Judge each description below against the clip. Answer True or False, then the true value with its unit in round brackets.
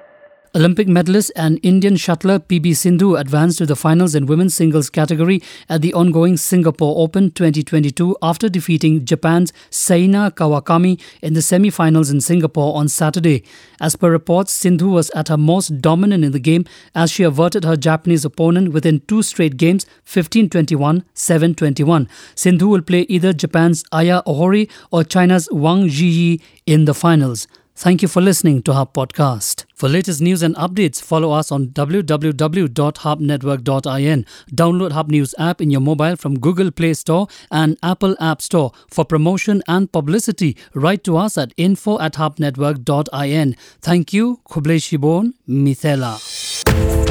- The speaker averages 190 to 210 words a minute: False (150 wpm)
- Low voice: False (165 Hz)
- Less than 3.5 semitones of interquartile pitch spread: True (2.9 semitones)